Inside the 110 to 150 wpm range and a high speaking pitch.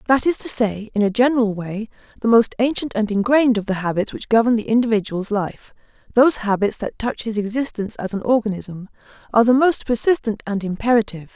No: average, 180 wpm; high, 220 Hz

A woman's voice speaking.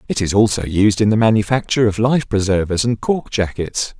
No: male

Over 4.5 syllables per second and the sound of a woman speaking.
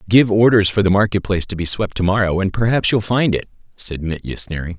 No: 6.0 syllables/s; male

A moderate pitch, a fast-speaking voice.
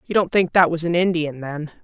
Yes: medium, 170 Hz; fast, 260 wpm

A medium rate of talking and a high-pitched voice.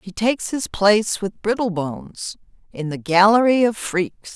Yes: average, 150 wpm; high, 200 Hz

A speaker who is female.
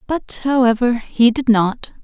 Yes: female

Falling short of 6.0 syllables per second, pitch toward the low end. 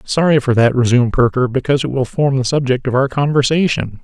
No: 6.1 syllables/s; low, 130 Hz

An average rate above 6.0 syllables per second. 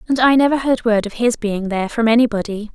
Yes: 6.2 syllables/s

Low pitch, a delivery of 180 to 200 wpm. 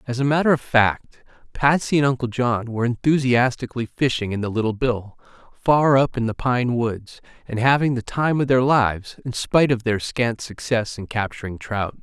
Yes: low, 120 Hz; average, 190 wpm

